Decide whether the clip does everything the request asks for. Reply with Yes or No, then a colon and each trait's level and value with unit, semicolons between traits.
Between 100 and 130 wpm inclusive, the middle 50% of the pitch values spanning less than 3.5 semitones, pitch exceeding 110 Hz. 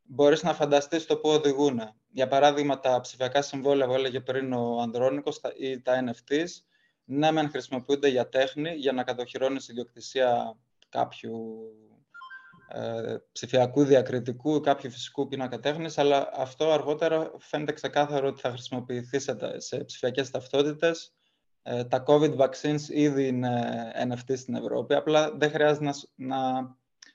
No: average, 140 wpm; average, 2.9 semitones; low, 135 Hz